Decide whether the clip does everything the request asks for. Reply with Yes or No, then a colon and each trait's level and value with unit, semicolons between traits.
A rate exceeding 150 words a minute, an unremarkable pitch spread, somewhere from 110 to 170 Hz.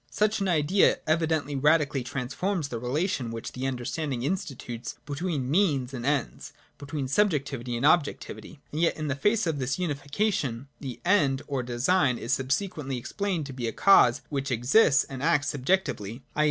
Yes: average, 165 wpm; average, 4.5 semitones; medium, 140 Hz